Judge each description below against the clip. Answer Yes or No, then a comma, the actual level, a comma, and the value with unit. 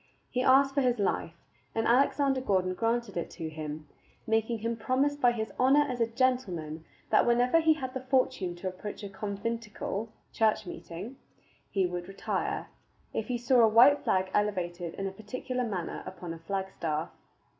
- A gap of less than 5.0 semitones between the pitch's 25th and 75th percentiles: No, wide, 5.4 semitones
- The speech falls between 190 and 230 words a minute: No, average, 170 wpm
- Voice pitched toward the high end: Yes, high, 220 Hz